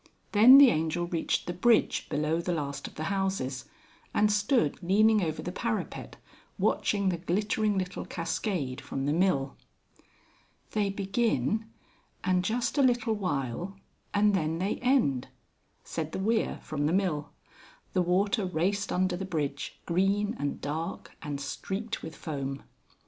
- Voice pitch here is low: No, medium, 185 Hz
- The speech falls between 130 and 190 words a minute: Yes, average, 145 wpm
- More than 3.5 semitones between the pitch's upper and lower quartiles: Yes, average, 5.1 semitones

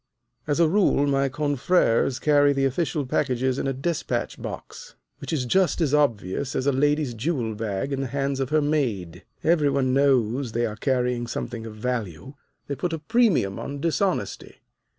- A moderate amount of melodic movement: Yes, average, 3.5 semitones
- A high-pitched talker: No, low, 135 Hz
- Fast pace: No, average, 175 wpm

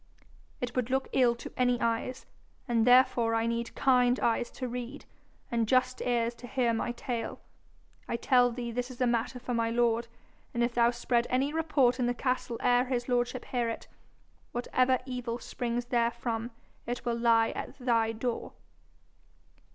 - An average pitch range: No, narrow, 1.2 semitones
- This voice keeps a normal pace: Yes, average, 170 wpm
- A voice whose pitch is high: Yes, high, 240 Hz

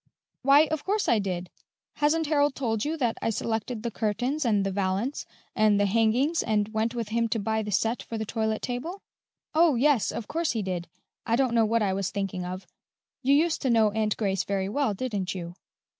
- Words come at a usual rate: No, fast, 210 wpm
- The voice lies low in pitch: No, high, 225 Hz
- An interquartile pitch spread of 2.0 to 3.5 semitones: No, average, 4.6 semitones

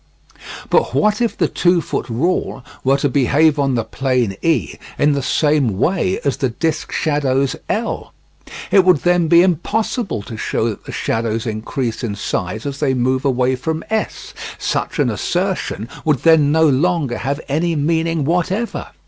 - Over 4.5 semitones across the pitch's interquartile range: Yes, average, 4.9 semitones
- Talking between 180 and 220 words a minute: No, average, 165 wpm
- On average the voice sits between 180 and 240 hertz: No, medium, 145 Hz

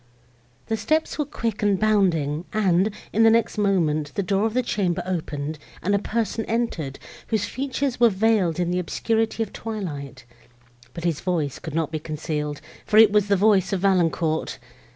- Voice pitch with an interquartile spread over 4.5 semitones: Yes, average, 5.3 semitones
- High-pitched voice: Yes, high, 195 Hz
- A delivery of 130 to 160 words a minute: No, average, 175 wpm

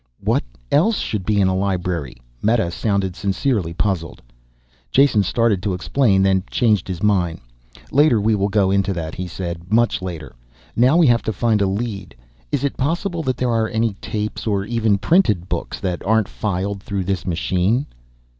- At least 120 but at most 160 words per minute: No, average, 175 wpm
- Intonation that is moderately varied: Yes, average, 3.8 semitones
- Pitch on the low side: Yes, low, 100 Hz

